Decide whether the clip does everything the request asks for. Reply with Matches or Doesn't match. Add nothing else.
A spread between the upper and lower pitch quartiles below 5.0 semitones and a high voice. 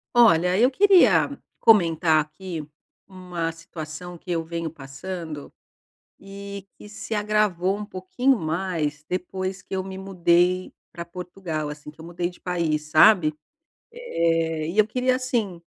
Doesn't match